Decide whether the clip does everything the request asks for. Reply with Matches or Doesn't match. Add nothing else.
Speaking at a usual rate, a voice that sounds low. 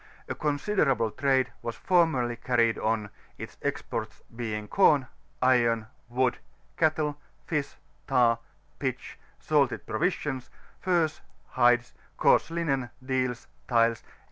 Doesn't match